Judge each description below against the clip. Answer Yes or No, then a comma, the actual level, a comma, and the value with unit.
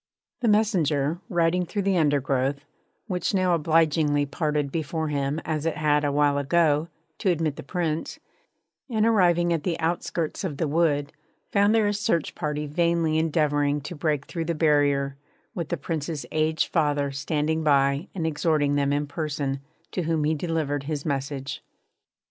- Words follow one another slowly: No, average, 160 wpm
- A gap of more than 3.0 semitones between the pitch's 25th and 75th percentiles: No, average, 2.7 semitones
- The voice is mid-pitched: Yes, medium, 155 Hz